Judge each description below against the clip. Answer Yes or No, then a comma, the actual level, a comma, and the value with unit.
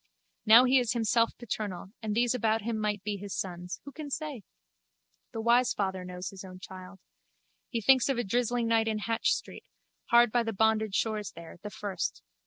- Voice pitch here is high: Yes, high, 220 Hz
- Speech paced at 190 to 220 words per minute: Yes, average, 195 wpm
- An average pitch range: Yes, average, 3.3 semitones